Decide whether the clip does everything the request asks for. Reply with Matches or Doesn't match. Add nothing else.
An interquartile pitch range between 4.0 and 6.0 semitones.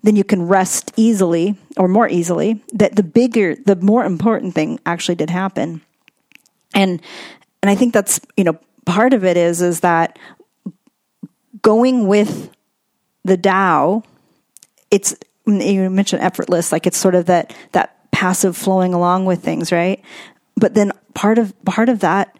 Doesn't match